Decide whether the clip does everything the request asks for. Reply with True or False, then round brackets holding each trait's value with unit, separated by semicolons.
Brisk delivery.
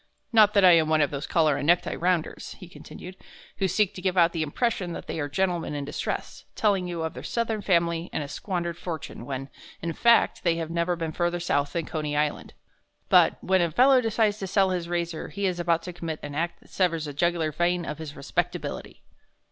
True (220 wpm)